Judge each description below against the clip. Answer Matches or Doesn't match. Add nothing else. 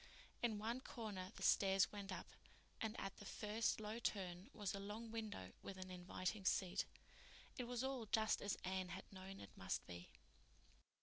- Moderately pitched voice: Doesn't match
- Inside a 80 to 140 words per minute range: Doesn't match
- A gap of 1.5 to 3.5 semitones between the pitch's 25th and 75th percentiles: Matches